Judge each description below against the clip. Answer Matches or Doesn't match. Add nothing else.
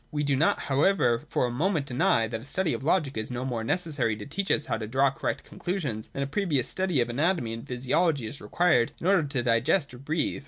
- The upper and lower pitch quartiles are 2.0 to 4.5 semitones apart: Doesn't match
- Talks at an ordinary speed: Doesn't match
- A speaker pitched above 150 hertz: Doesn't match